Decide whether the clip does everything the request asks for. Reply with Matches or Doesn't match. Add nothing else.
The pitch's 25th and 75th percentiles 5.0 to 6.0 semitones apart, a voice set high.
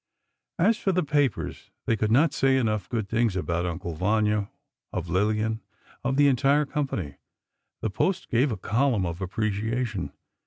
Doesn't match